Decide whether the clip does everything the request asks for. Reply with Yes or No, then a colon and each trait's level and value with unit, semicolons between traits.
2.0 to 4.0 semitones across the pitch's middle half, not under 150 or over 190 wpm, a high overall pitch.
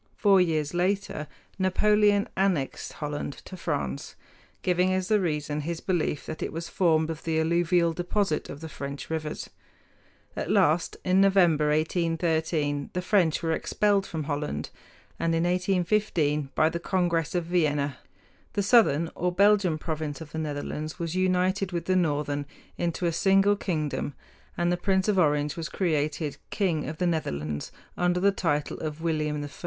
No: average, 3.4 semitones; average, 160 wpm; medium, 165 Hz